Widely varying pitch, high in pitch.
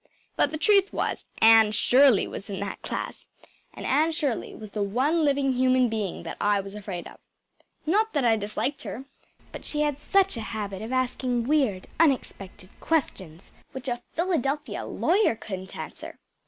Yes: wide, 6.2 semitones; very high, 250 Hz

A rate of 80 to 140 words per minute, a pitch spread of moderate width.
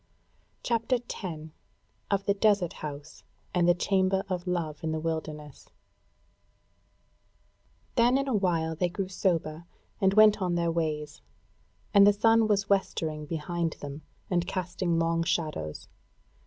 Yes: slow, 135 wpm; average, 3.9 semitones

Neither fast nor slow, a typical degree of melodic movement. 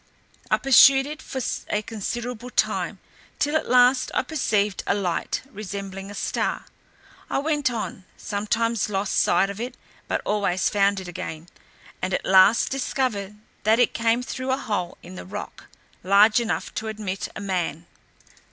Yes: average, 160 wpm; average, 4.1 semitones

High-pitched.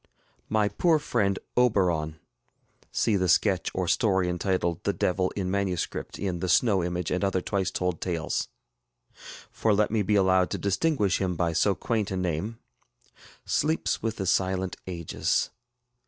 No: very low, 95 Hz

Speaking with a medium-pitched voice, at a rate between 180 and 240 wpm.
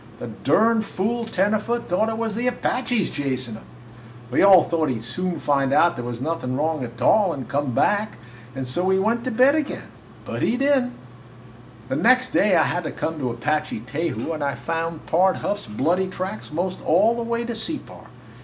Yes: medium, 180 Hz; average, 200 wpm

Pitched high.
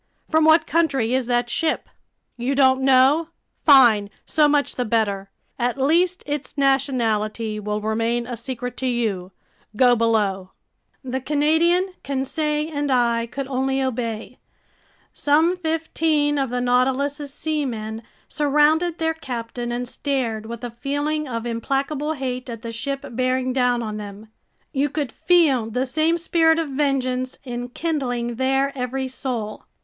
Yes: very high, 260 Hz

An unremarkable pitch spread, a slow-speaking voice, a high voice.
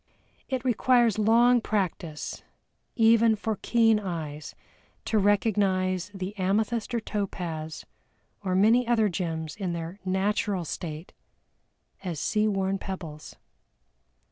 Yes: average, 3.8 semitones; slow, 110 wpm; high, 200 Hz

